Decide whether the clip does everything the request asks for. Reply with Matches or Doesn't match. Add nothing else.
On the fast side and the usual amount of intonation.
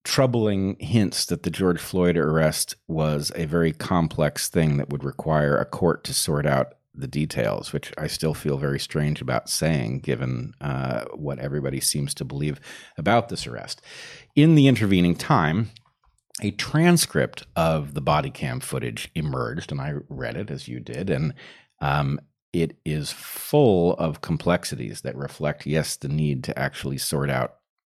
Doesn't match